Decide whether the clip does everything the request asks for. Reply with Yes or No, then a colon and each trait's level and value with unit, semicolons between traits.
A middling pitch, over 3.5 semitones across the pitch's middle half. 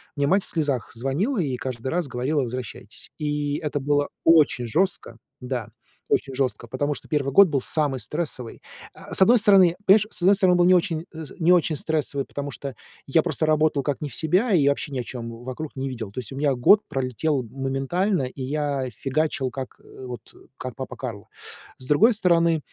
Yes: medium, 145 Hz; average, 4.1 semitones